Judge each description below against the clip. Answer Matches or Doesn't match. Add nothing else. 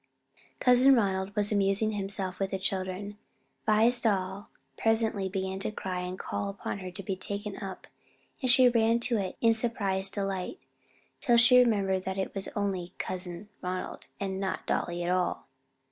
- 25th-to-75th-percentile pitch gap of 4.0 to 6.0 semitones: Doesn't match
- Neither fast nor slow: Matches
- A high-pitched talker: Matches